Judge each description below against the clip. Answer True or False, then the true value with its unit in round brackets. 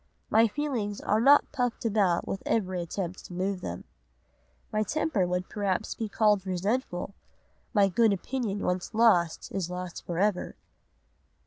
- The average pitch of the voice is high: True (200 Hz)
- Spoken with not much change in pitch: False (3.7 semitones)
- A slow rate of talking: False (145 wpm)